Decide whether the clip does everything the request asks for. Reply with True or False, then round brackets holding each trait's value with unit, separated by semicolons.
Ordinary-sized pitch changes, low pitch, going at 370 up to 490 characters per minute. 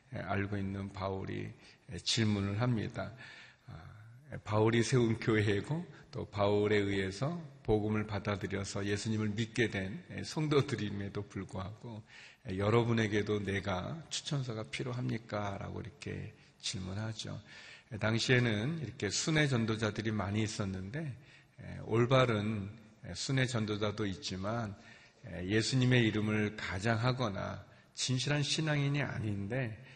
False (3.5 semitones; 110 Hz; 265 characters per minute)